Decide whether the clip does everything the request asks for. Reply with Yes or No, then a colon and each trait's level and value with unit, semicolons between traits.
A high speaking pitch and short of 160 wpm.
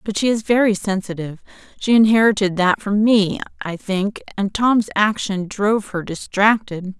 Yes: high, 205 Hz; slow, 135 wpm